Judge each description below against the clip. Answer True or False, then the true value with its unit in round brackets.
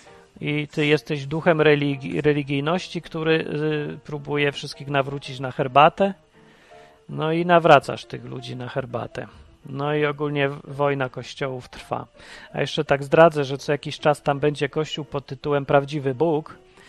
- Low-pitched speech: False (145 Hz)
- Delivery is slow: False (145 wpm)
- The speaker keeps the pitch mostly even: True (1.6 semitones)